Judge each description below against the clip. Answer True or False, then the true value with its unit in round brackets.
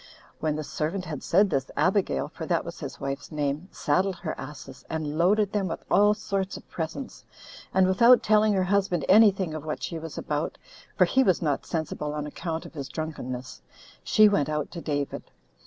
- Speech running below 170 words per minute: False (190 wpm)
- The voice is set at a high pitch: False (165 Hz)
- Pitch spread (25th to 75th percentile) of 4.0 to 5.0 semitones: True (4.5 semitones)